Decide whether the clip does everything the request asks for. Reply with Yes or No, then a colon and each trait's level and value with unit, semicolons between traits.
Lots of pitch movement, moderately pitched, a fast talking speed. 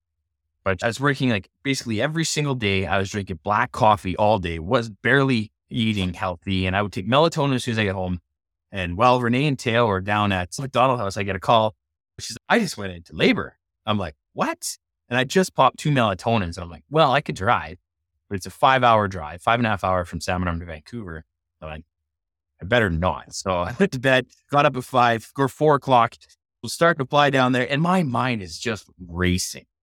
No: wide, 6.1 semitones; low, 105 Hz; fast, 230 wpm